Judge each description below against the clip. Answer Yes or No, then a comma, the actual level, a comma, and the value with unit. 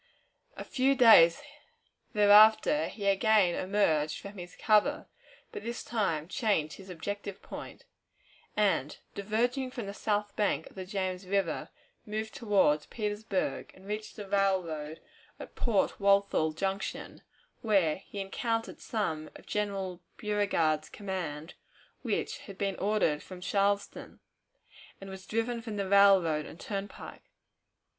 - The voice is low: No, high, 200 Hz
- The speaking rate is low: Yes, slow, 130 wpm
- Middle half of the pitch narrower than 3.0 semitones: Yes, narrow, 2.6 semitones